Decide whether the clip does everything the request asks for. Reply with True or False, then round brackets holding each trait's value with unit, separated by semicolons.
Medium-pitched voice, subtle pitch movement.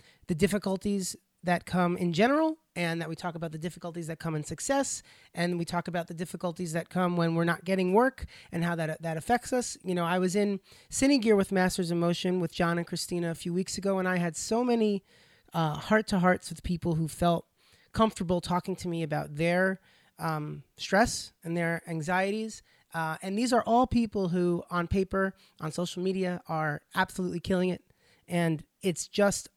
True (180 Hz; 2.3 semitones)